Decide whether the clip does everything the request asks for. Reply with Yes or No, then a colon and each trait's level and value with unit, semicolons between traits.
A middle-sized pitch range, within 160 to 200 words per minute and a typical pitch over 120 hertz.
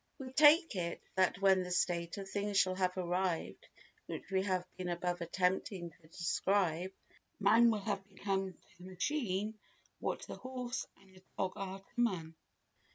No: narrow, 2.2 semitones; average, 165 wpm; high, 190 Hz